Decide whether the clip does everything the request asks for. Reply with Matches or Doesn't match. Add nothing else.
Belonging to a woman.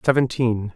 Doesn't match